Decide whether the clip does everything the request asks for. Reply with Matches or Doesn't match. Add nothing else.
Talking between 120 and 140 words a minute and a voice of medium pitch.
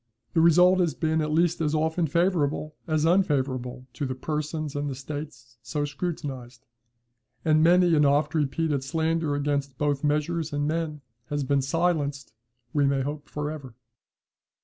Doesn't match